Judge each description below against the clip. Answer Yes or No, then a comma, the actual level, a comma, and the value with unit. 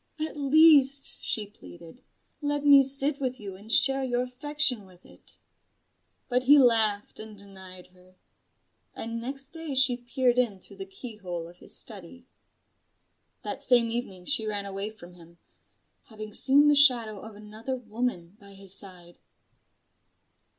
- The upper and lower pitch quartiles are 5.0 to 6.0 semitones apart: Yes, wide, 5.4 semitones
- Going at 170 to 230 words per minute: No, average, 150 wpm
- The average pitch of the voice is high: Yes, high, 230 Hz